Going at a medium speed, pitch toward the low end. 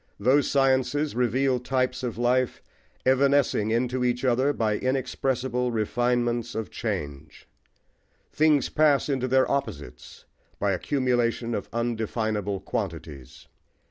No: slow, 110 wpm; low, 125 Hz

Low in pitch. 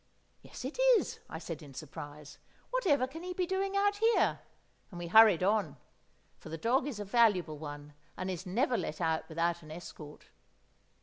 No: medium, 185 Hz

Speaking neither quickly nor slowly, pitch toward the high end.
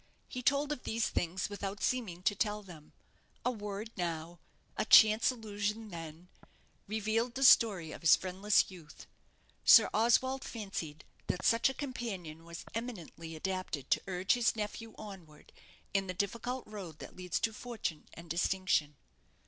Yes: average, 150 wpm; high, 200 Hz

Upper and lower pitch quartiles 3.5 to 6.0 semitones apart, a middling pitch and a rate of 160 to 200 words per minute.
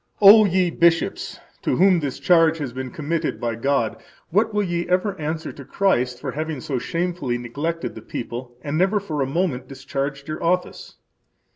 Yes: average, 5.1 semitones; medium, 155 Hz; average, 175 wpm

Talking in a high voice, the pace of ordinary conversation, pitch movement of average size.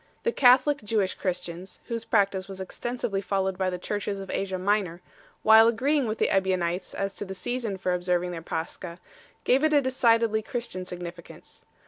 Yes: high, 195 Hz; average, 170 wpm; average, 4.0 semitones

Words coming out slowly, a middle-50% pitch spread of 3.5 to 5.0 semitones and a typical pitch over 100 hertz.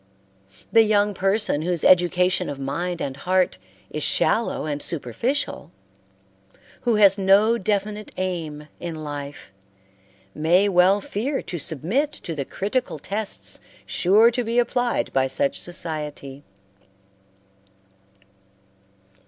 No: slow, 110 wpm; wide, 5.5 semitones; medium, 185 Hz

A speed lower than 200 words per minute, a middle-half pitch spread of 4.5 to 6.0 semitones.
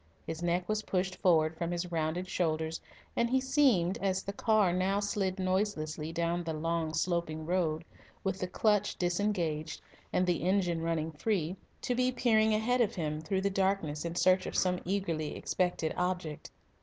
No: average, 170 wpm; average, 3.3 semitones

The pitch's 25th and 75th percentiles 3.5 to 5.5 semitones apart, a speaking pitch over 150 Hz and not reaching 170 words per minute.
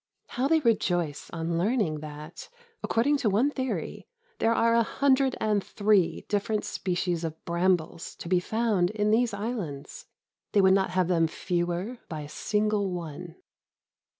Yes: average, 4.7 semitones; high, 190 Hz; average, 150 wpm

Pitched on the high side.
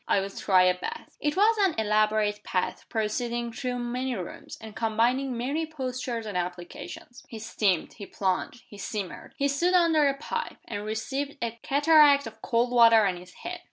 Yes: high, 235 Hz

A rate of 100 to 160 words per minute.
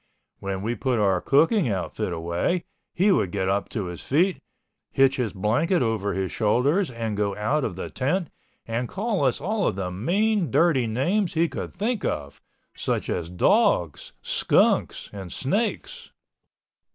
Yes: average, 155 wpm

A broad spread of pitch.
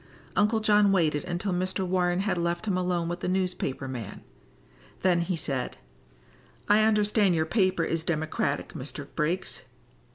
No: average, 2.9 semitones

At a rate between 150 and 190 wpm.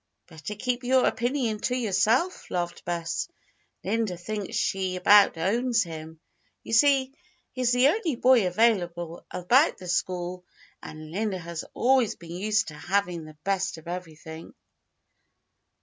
No: slow, 135 wpm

